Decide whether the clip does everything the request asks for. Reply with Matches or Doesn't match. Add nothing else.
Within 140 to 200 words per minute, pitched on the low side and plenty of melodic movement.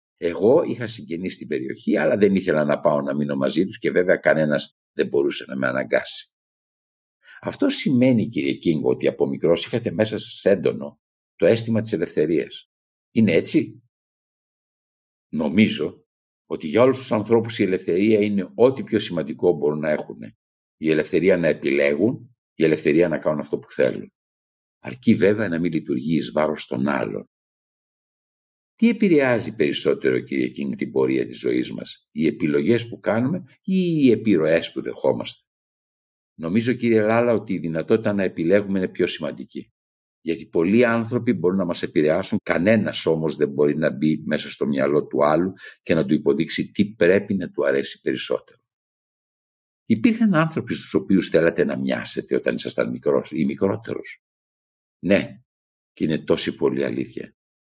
Matches